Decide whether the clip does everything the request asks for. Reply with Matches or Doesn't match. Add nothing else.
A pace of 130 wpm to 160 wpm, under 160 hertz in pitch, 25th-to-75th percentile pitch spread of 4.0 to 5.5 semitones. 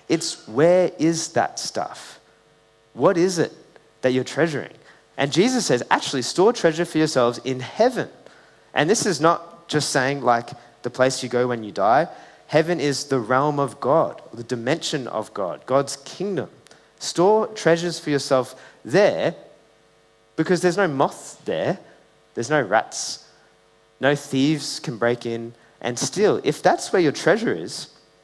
Matches